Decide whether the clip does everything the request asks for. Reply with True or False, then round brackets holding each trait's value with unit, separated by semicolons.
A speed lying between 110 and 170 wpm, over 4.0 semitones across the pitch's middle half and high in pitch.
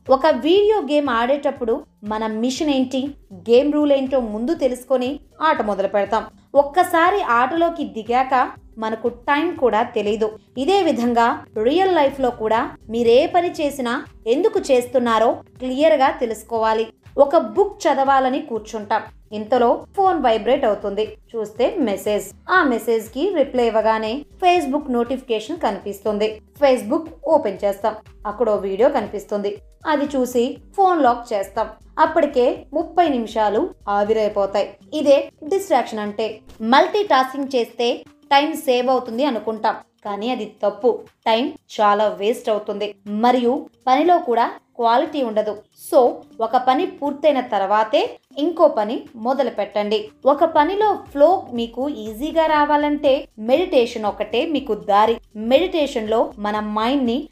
True (120 wpm; 5.1 semitones; 250 Hz)